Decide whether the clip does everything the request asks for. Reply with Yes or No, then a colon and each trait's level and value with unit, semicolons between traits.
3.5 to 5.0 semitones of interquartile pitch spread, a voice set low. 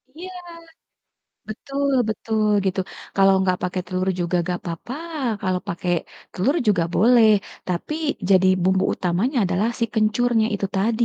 No: average, 4.0 semitones; high, 195 Hz